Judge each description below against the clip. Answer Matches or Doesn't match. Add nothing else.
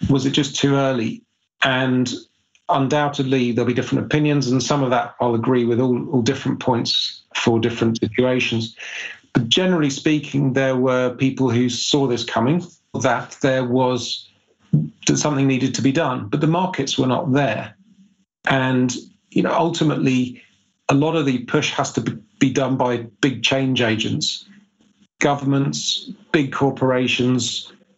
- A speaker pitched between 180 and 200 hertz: Doesn't match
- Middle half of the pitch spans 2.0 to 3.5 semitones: Matches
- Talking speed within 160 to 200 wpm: Doesn't match